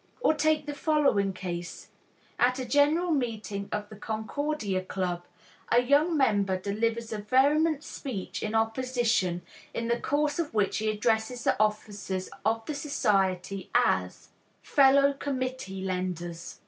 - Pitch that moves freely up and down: Yes, wide, 6.0 semitones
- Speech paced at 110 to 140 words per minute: Yes, slow, 135 wpm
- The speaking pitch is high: Yes, high, 225 Hz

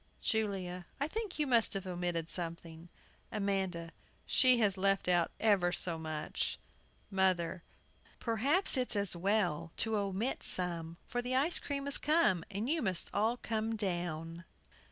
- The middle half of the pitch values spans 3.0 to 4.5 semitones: No, average, 4.9 semitones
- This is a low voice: No, high, 195 Hz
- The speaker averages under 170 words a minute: Yes, average, 145 wpm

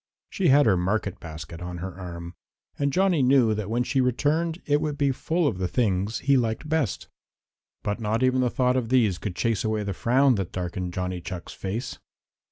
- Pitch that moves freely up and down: Yes, wide, 6.4 semitones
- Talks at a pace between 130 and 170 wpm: No, average, 200 wpm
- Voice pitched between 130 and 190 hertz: No, low, 115 Hz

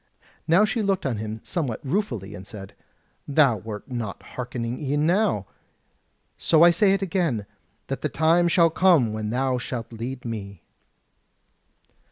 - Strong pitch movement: Yes, wide, 7.5 semitones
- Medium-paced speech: Yes, average, 150 wpm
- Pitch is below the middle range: Yes, low, 130 Hz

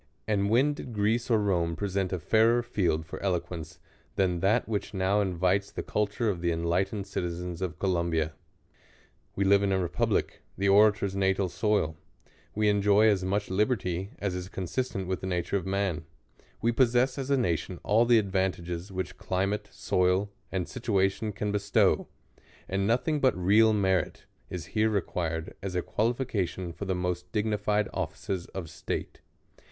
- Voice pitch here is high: No, very low, 95 Hz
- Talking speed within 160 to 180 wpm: Yes, average, 165 wpm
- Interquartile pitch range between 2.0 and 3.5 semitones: Yes, average, 2.8 semitones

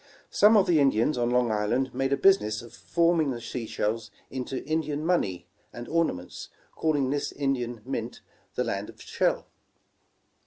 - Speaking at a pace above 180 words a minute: No, average, 165 wpm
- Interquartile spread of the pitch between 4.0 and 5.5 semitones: Yes, average, 5.0 semitones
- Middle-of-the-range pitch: No, low, 130 Hz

